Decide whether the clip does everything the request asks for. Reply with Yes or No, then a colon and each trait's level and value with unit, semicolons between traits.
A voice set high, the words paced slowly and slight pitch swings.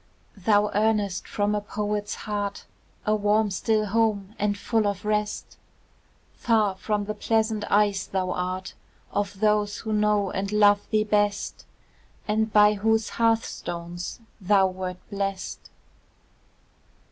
Yes: high, 210 Hz; slow, 125 wpm; narrow, 1.2 semitones